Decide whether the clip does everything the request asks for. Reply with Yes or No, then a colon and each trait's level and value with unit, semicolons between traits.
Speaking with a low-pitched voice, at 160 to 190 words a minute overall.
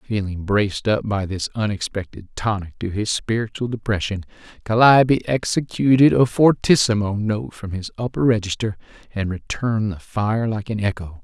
No: low, 105 Hz; average, 145 wpm